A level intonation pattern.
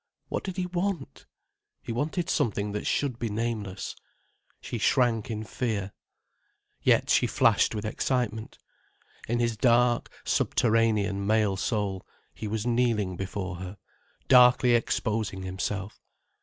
No: average, 3.2 semitones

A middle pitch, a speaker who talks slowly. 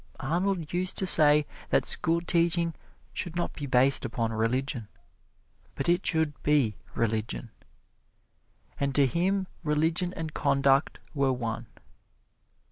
Yes: medium, 150 Hz; slow, 120 wpm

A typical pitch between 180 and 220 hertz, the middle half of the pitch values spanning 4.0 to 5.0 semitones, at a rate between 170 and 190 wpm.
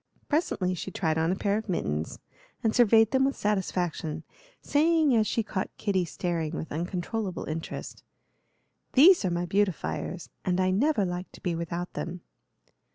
No: medium, 185 Hz; average, 4.3 semitones; average, 160 wpm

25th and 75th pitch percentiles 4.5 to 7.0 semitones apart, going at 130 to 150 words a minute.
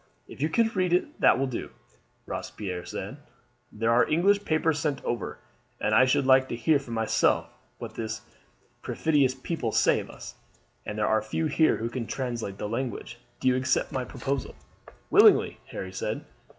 No: average, 5.1 semitones; average, 175 wpm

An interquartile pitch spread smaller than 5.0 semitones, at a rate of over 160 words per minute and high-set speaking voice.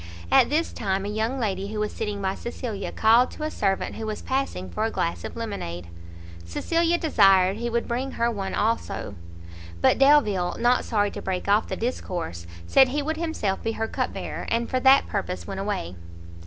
Yes: average, 4.6 semitones; average, 195 wpm; high, 215 Hz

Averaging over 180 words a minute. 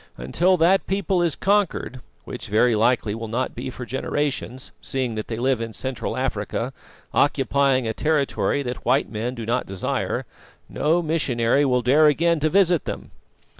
No: average, 165 wpm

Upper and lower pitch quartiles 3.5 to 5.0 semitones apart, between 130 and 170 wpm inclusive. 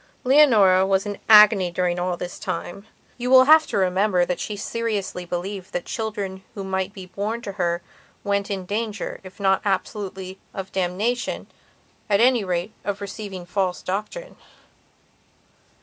No: narrow, 2.5 semitones; average, 150 wpm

